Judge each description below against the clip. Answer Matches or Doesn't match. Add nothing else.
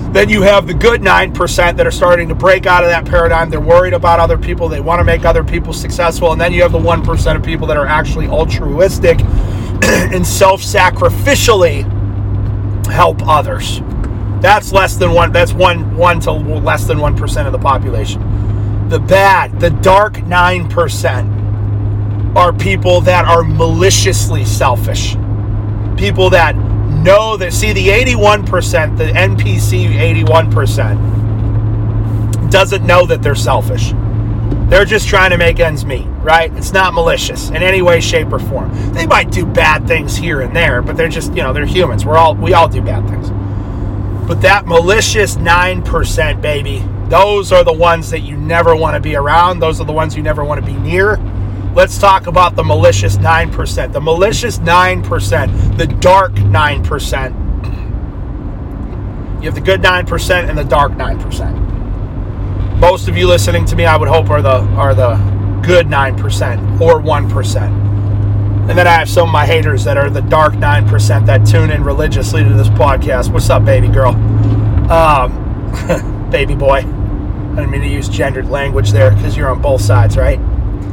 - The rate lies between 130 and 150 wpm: Doesn't match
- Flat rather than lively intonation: Matches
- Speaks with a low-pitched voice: Matches